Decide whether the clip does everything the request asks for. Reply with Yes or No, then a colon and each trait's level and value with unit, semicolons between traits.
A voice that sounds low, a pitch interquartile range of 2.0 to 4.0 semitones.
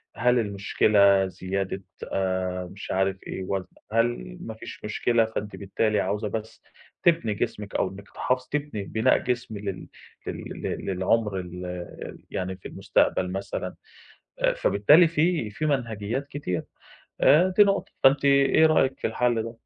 No: low, 105 Hz; average, 4.6 semitones